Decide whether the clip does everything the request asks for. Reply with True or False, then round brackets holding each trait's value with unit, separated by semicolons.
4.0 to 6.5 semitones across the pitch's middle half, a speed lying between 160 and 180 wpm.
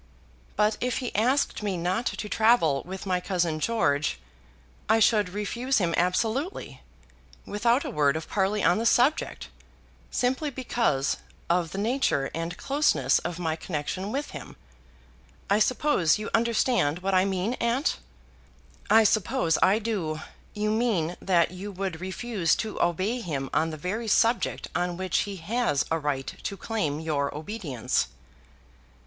False (5.6 semitones; 150 wpm)